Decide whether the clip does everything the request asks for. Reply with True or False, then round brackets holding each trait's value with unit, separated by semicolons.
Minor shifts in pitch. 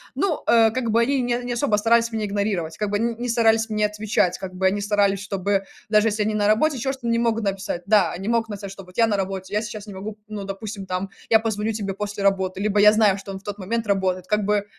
True (2.3 semitones)